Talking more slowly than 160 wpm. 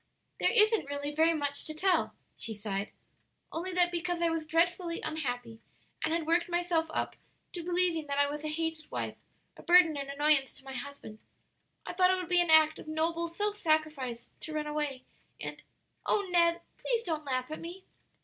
No: average, 190 wpm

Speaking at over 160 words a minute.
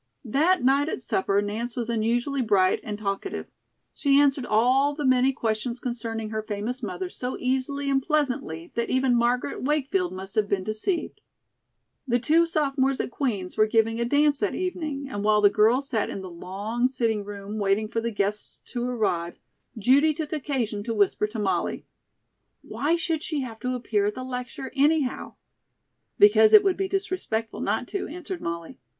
Yes: average, 175 wpm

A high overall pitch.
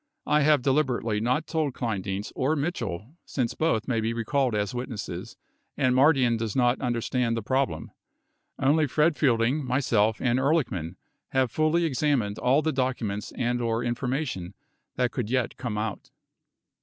No: low, 125 Hz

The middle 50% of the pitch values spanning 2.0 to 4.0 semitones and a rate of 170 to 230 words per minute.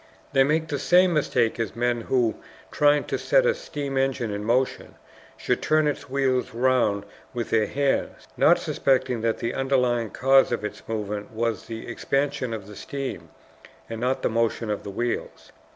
Yes: average, 3.4 semitones; average, 175 wpm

